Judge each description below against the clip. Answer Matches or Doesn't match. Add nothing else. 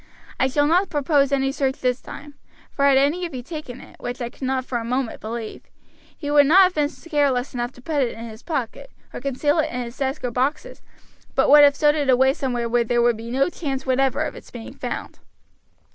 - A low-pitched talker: Doesn't match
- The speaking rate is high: Matches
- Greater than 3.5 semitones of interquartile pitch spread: Doesn't match